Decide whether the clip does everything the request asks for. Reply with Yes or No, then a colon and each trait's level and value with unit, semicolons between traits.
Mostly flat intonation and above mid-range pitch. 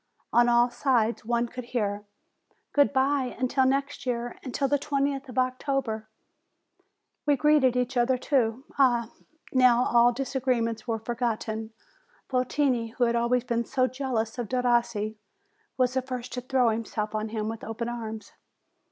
Yes: narrow, 2.3 semitones; high, 245 Hz